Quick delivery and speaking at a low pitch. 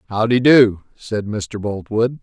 No: average, 160 wpm; low, 110 Hz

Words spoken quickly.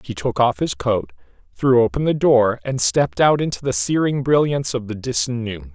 Yes: fast, 210 wpm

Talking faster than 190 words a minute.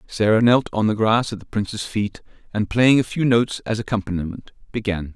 Yes: average, 200 wpm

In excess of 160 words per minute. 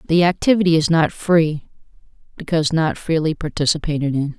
No: slow, 135 wpm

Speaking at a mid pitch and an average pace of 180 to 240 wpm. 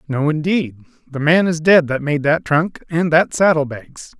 Yes: medium, 155 Hz; average, 200 wpm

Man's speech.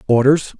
Yes: male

